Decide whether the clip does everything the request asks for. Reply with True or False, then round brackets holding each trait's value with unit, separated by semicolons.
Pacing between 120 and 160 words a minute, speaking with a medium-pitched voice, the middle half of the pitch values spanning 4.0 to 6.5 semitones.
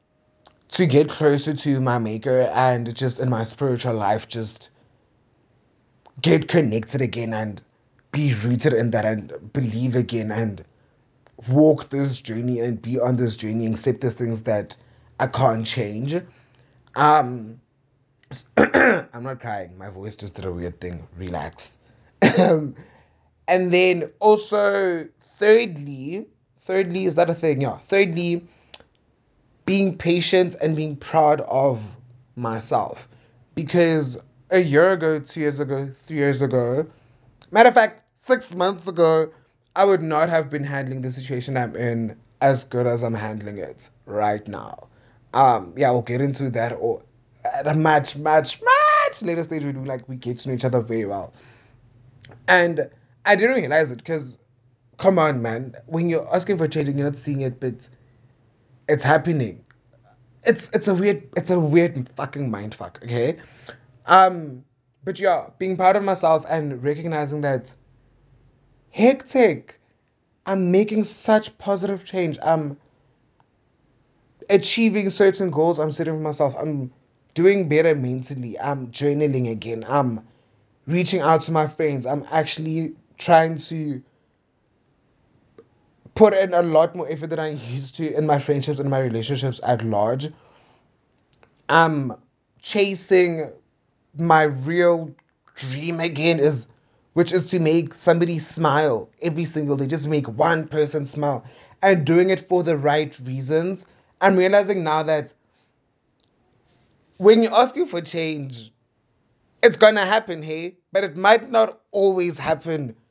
True (145 wpm; 145 Hz; 5.5 semitones)